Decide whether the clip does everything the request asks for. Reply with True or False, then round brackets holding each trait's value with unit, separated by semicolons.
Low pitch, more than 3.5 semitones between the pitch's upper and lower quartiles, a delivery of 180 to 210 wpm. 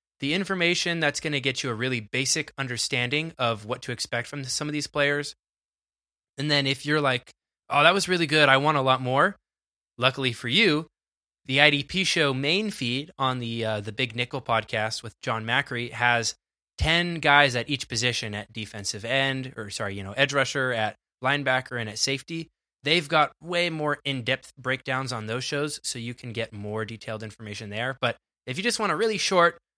True (130 Hz; 3.9 semitones; 200 wpm)